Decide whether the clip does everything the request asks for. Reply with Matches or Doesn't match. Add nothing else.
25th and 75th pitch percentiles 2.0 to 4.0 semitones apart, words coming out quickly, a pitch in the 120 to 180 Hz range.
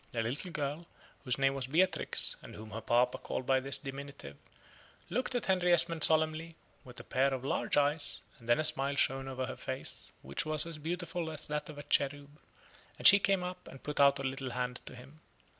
Matches